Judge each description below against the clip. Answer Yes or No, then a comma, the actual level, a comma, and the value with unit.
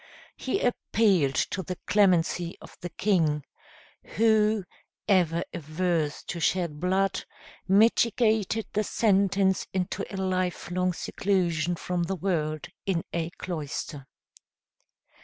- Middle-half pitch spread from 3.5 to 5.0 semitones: No, average, 2.9 semitones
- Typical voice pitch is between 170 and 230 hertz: Yes, medium, 185 Hz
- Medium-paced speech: No, slow, 105 wpm